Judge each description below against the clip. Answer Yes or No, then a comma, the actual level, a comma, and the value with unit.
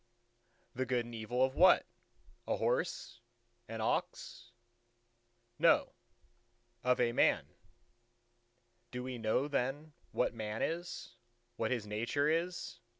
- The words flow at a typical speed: No, slow, 115 wpm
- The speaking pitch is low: Yes, low, 125 Hz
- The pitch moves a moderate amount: Yes, average, 3.5 semitones